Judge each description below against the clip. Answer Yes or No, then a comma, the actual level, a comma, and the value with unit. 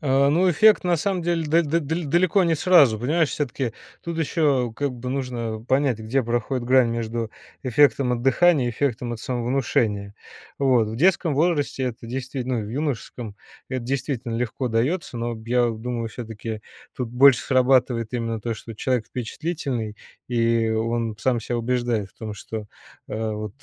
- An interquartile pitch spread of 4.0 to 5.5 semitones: No, average, 3.6 semitones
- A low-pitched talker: Yes, low, 125 Hz